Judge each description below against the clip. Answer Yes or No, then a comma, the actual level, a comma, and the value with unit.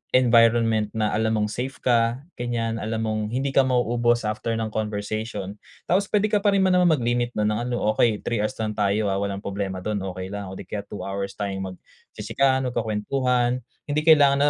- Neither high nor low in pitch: No, low, 115 Hz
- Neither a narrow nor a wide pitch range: Yes, average, 3.2 semitones